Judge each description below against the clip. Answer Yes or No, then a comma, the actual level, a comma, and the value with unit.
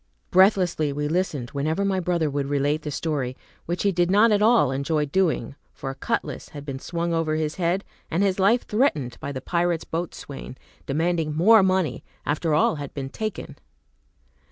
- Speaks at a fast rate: No, average, 180 wpm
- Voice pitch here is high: No, medium, 160 Hz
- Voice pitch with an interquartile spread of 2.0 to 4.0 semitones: No, average, 4.5 semitones